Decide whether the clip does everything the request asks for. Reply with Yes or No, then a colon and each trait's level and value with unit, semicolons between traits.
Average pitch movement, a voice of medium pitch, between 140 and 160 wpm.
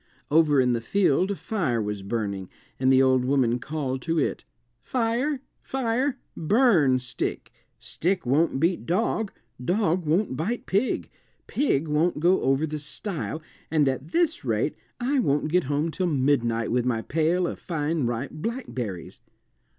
No: wide, 6.6 semitones; medium, 155 Hz; average, 150 wpm